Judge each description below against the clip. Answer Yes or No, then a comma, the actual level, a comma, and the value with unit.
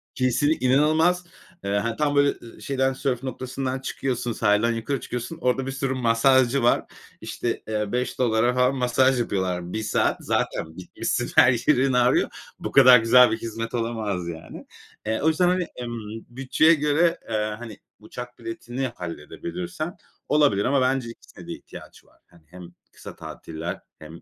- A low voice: Yes, low, 125 Hz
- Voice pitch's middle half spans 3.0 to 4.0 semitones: Yes, average, 3.3 semitones